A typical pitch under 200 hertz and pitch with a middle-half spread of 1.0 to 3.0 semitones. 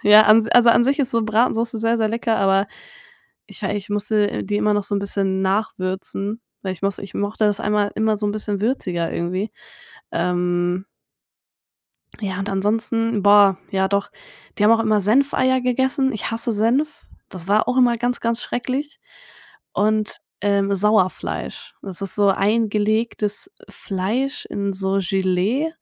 No: high, 210 Hz; average, 2.7 semitones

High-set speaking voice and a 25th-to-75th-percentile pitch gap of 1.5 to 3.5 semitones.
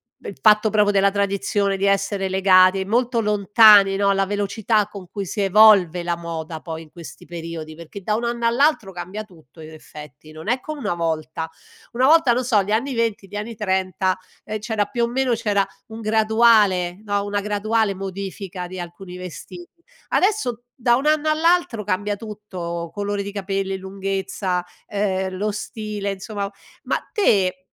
Yes: high, 200 Hz; average, 2.8 semitones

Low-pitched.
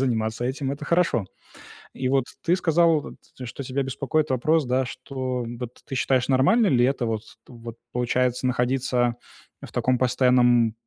Yes: low, 130 Hz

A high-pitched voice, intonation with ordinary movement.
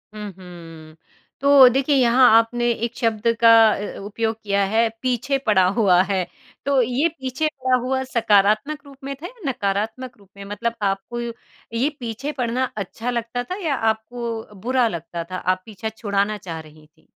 Yes: high, 230 Hz; average, 4.2 semitones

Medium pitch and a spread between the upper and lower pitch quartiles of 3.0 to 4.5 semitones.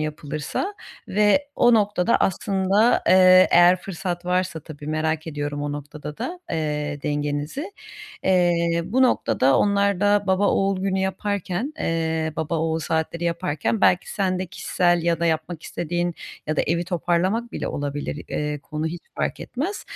Yes: medium, 175 Hz; average, 3.8 semitones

